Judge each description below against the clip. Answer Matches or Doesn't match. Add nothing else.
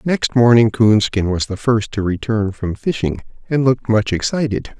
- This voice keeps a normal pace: Matches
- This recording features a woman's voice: Doesn't match